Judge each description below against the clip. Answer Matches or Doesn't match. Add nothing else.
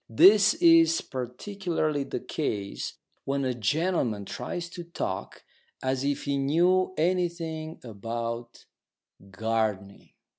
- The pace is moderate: Doesn't match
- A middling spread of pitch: Doesn't match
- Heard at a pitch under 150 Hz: Matches